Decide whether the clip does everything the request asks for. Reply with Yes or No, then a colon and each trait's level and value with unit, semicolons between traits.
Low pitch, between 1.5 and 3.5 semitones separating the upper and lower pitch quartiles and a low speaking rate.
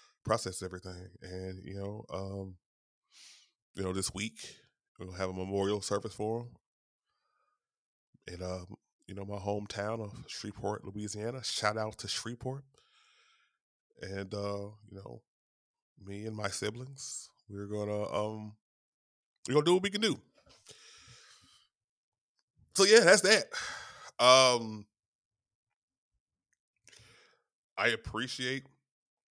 Yes: low, 105 Hz; average, 2.9 semitones; slow, 120 wpm